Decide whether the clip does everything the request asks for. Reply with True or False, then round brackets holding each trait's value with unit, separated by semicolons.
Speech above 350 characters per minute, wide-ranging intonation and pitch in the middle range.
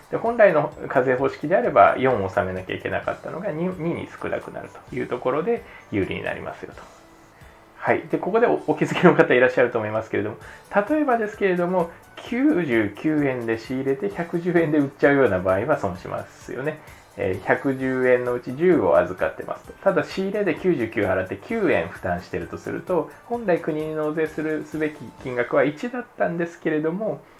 True (360 characters per minute; 6.5 semitones; 155 Hz)